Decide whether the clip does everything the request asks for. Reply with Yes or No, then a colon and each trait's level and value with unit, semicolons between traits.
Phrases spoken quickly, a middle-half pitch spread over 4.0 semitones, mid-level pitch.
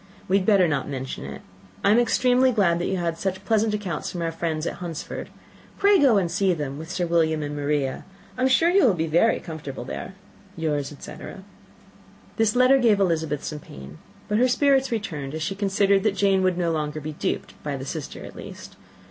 Yes: fast, 210 wpm; wide, 5.5 semitones; medium, 175 Hz